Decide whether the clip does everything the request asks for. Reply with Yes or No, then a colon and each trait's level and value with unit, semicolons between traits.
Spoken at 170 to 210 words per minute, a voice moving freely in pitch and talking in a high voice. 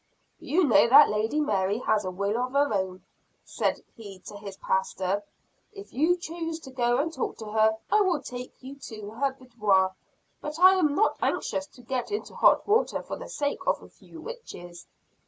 Yes: average, 190 wpm; wide, 6.7 semitones; very high, 250 Hz